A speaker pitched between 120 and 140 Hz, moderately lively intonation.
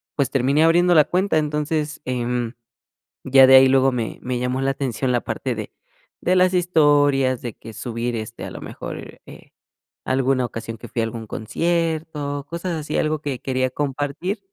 Yes: low, 135 Hz; average, 3.7 semitones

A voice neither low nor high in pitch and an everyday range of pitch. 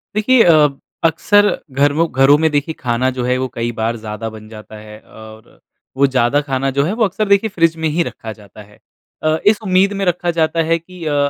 No: medium, 145 Hz; wide, 6.6 semitones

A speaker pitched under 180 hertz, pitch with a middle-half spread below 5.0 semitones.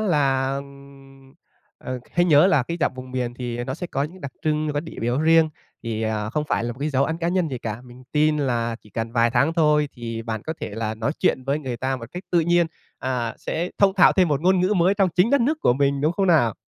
No: medium, 140 Hz; average, 5.3 semitones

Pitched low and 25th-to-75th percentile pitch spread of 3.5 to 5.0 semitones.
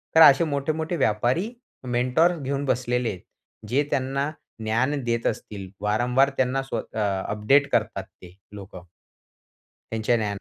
Yes: low, 125 Hz; average, 4.5 semitones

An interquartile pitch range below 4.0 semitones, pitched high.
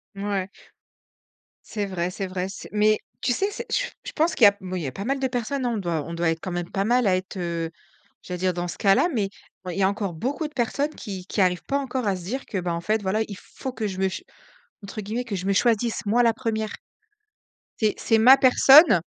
No: average, 4.7 semitones; high, 200 Hz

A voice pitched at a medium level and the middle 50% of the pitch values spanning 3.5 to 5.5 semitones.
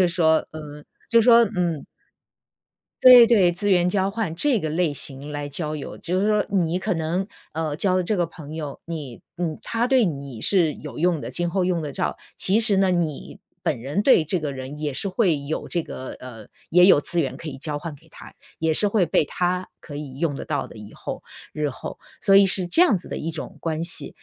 Yes: medium, 165 Hz; average, 4.1 semitones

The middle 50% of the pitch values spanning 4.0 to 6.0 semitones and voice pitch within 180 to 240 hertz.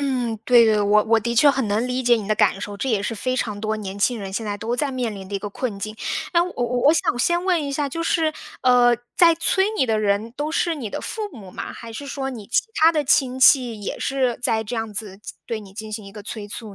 Yes: average, 4.3 semitones; high, 235 Hz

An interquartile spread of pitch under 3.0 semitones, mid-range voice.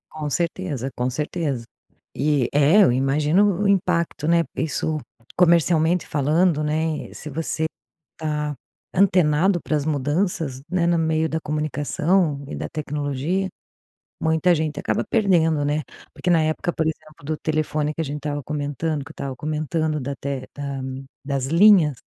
Yes: narrow, 2.5 semitones; medium, 155 Hz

